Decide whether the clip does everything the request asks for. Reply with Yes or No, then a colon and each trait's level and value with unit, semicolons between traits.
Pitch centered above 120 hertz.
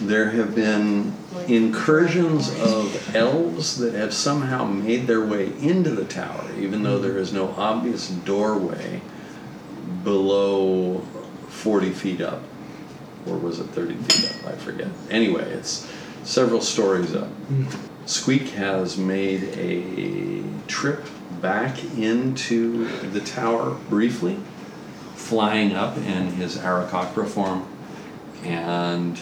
No: low, 105 Hz